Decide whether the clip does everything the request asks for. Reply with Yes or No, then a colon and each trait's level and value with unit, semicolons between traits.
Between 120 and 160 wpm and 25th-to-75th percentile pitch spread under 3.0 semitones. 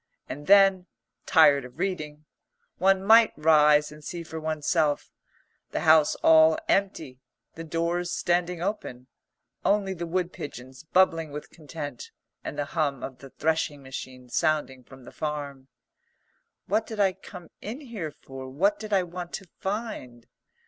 No: average, 150 wpm; average, 4.3 semitones